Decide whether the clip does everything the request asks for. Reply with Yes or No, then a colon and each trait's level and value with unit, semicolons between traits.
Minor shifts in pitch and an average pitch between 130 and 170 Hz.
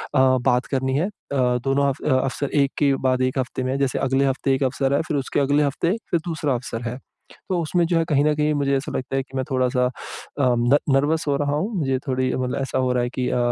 Yes: narrow, 2.0 semitones; low, 135 Hz